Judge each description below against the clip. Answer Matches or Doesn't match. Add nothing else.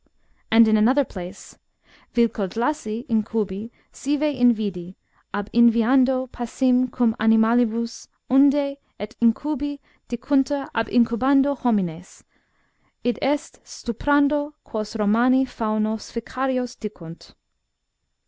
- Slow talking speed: Matches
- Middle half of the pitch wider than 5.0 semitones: Doesn't match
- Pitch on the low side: Doesn't match